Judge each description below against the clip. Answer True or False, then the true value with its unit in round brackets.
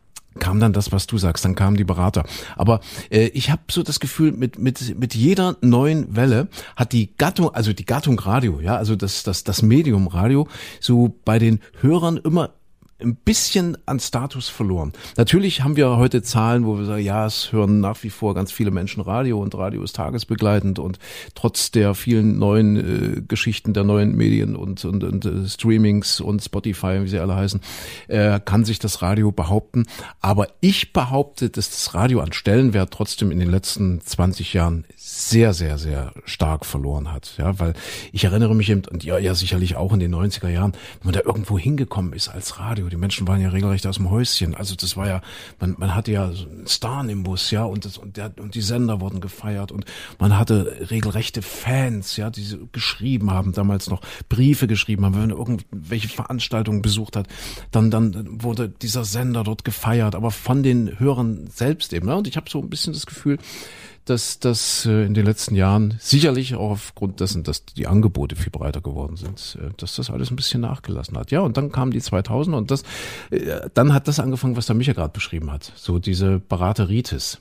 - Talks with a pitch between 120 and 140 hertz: False (105 Hz)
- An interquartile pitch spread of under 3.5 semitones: False (4.0 semitones)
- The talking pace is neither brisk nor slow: False (200 wpm)